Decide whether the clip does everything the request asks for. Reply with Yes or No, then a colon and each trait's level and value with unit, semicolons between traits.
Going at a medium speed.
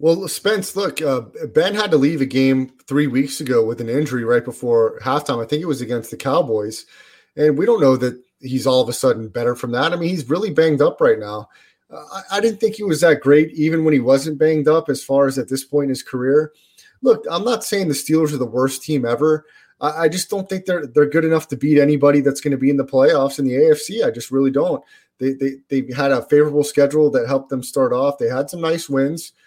No: fast, 255 wpm